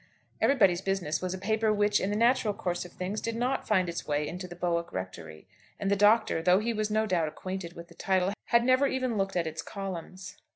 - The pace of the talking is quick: Yes, fast, 225 wpm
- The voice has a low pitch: No, high, 190 Hz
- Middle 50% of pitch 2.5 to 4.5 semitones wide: Yes, average, 3.7 semitones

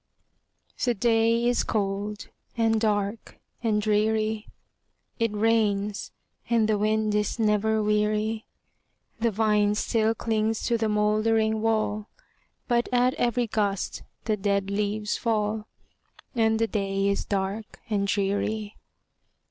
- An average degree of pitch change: No, narrow, 1.3 semitones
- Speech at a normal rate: No, slow, 120 wpm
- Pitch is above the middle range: Yes, high, 215 Hz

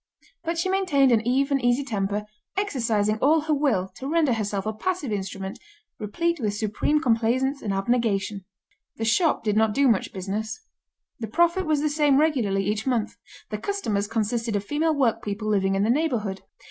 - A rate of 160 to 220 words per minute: Yes, average, 170 wpm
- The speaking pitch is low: No, high, 230 Hz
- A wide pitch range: Yes, wide, 5.9 semitones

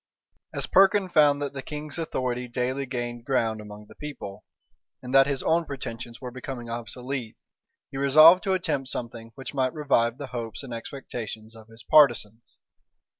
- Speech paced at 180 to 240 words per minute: No, average, 165 wpm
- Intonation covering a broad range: No, average, 3.5 semitones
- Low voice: Yes, low, 130 Hz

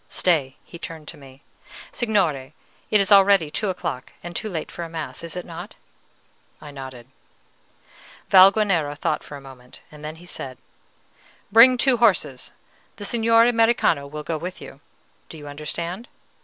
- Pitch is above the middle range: No, medium, 165 Hz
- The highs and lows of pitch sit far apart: Yes, wide, 5.7 semitones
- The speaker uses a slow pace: No, average, 150 wpm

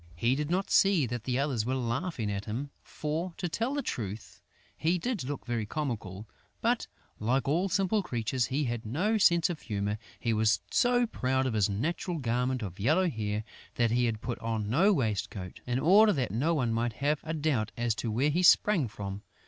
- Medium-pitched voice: No, low, 125 Hz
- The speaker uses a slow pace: No, average, 200 wpm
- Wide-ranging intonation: Yes, wide, 6.8 semitones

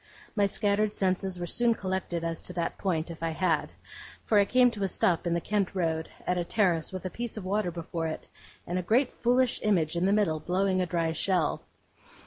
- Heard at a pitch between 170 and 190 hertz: Yes, medium, 185 Hz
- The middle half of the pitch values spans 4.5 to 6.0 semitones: No, average, 3.4 semitones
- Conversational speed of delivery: No, fast, 220 wpm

